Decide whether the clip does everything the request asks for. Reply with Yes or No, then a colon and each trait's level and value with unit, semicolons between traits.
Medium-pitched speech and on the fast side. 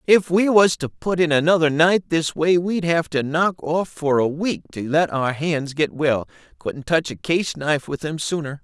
Yes: medium, 160 Hz; fast, 220 wpm